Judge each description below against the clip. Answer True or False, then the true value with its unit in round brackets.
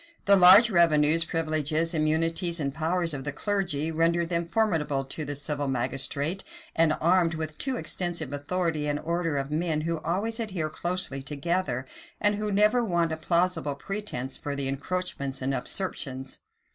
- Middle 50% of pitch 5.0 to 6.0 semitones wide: False (3.8 semitones)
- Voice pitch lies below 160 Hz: False (165 Hz)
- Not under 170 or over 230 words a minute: False (160 wpm)